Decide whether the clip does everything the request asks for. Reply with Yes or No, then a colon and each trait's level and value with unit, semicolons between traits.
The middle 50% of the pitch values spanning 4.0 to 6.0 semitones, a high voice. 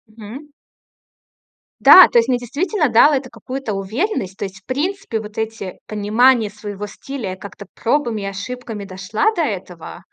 Yes: average, 4.6 semitones; high, 225 Hz